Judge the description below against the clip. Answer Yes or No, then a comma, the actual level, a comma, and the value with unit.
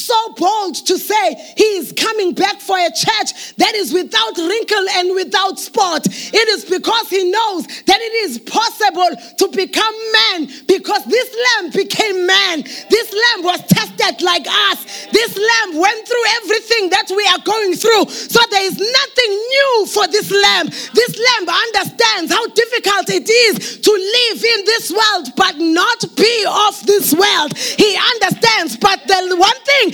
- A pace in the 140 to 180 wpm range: Yes, average, 165 wpm